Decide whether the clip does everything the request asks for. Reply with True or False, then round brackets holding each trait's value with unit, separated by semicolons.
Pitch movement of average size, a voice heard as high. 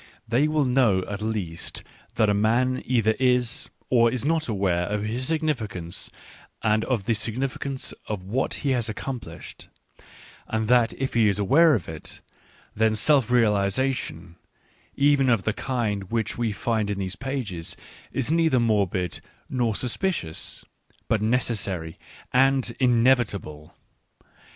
False (4.1 semitones; 115 Hz)